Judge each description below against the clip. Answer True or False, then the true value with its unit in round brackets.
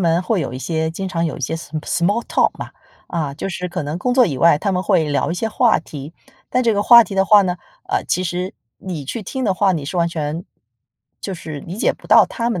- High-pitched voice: False (175 Hz)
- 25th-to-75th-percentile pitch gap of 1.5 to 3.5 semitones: False (3.9 semitones)